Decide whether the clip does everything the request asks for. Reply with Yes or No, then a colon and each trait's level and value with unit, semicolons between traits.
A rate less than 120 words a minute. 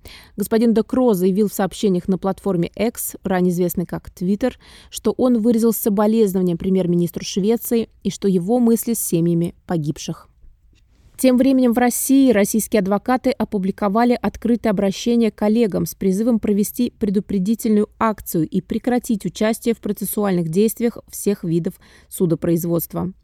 No: average, 125 wpm